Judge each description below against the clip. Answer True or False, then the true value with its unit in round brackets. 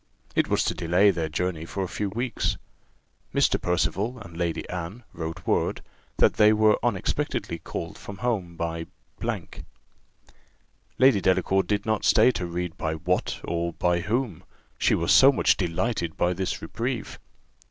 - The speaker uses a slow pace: False (150 wpm)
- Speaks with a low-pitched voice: True (90 Hz)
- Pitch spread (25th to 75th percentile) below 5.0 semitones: True (4.1 semitones)